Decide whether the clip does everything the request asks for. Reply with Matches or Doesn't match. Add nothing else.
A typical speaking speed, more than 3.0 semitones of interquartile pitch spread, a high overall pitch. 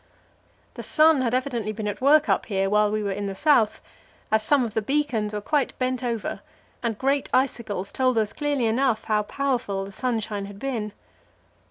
Matches